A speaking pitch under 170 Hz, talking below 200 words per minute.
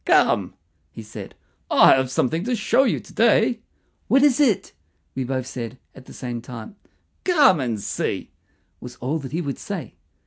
Yes: medium, 140 Hz; average, 175 wpm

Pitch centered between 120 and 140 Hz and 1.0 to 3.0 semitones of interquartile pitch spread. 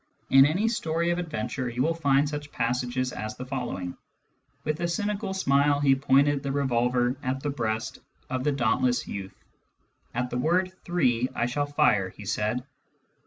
No: low, 135 Hz; average, 3.4 semitones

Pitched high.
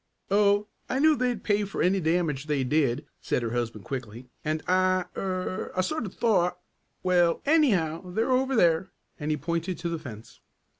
No: medium, 180 Hz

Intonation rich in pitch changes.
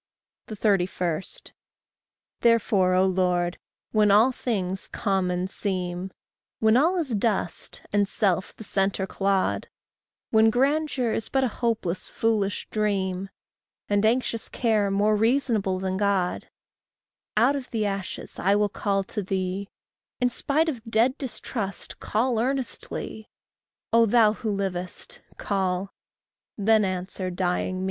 No: average, 3.3 semitones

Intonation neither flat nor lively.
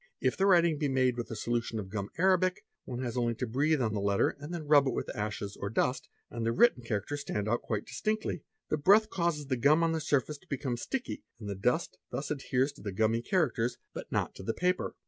No: wide, 5.8 semitones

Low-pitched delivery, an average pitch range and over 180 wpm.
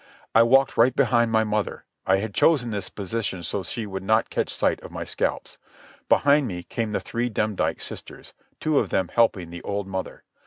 Yes: low, 110 Hz; average, 3.5 semitones; average, 200 wpm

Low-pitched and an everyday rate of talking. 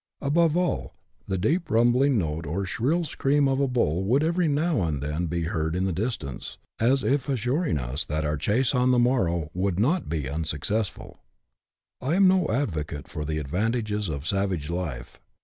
Yes: low, 105 Hz; average, 180 wpm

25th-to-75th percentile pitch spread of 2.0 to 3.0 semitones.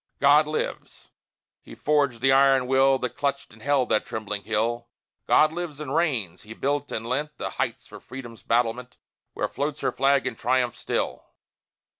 No: average, 3.5 semitones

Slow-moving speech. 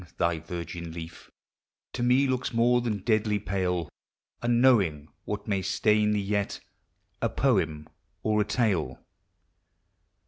Yes: slow, 125 wpm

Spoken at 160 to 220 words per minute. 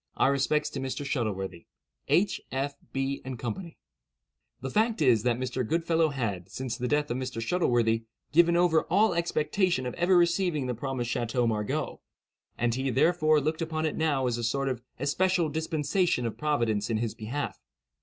Yes: average, 175 wpm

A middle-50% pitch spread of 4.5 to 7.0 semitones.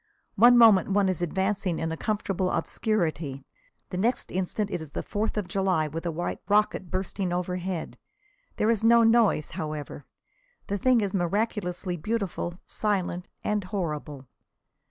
No: average, 3.5 semitones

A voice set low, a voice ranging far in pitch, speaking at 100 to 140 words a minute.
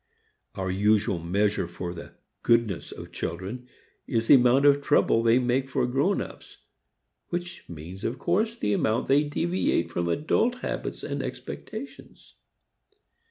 Yes: low, 120 Hz; wide, 6.9 semitones; slow, 135 wpm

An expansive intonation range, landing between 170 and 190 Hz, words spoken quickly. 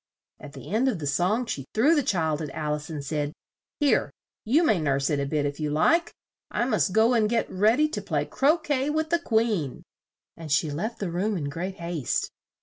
Yes: wide, 8.3 semitones; medium, 185 Hz; fast, 225 wpm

